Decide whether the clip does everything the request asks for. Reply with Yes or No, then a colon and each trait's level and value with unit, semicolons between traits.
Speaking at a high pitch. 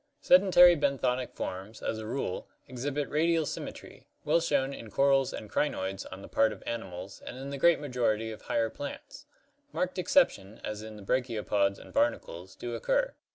No: low, 130 Hz